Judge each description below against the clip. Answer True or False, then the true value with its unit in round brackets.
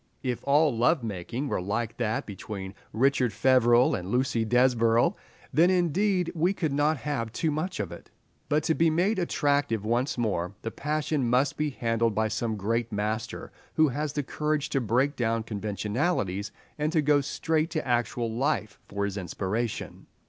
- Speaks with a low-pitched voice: True (125 Hz)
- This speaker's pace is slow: False (165 wpm)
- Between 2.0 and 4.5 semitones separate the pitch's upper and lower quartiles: False (5.4 semitones)